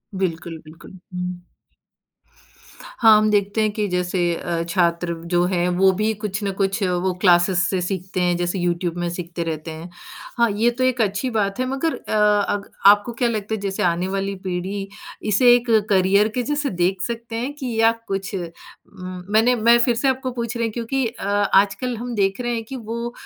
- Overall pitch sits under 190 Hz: No, high, 200 Hz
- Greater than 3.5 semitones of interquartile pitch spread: Yes, average, 4.4 semitones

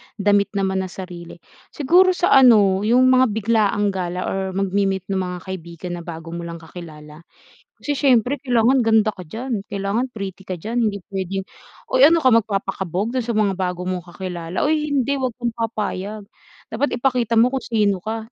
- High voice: Yes, high, 205 Hz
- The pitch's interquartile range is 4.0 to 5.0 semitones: Yes, average, 4.5 semitones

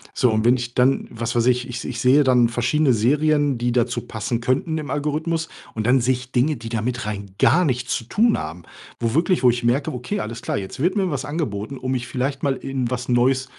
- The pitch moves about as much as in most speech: Yes, average, 3.2 semitones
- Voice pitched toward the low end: Yes, low, 125 Hz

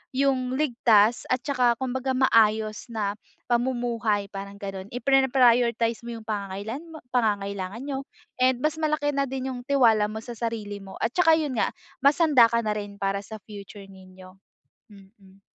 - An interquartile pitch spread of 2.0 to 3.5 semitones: No, average, 4.3 semitones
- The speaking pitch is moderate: No, high, 230 Hz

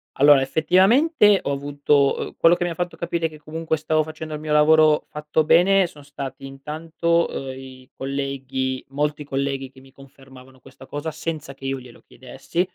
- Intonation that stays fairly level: No, average, 3.0 semitones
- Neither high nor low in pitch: Yes, medium, 145 Hz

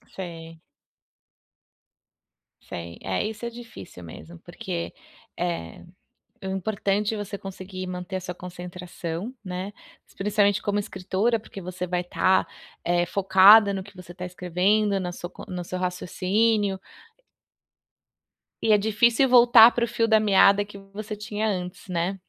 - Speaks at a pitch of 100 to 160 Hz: No, high, 190 Hz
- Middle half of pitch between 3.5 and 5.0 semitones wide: No, average, 2.8 semitones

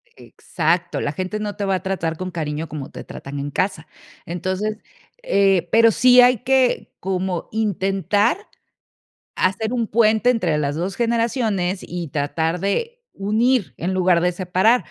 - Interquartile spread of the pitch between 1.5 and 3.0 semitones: No, average, 4.3 semitones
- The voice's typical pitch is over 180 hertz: Yes, high, 190 Hz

